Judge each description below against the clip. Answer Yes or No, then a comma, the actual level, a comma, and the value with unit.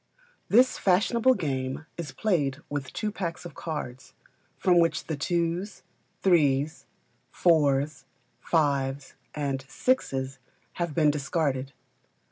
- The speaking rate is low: Yes, slow, 105 wpm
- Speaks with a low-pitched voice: No, medium, 155 Hz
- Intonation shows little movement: No, average, 4.2 semitones